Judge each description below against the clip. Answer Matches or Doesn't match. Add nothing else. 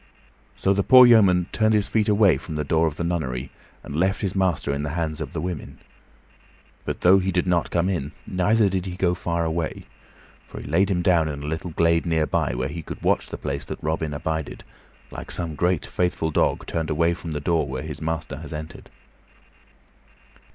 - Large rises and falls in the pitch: Doesn't match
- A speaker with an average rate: Doesn't match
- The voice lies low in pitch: Matches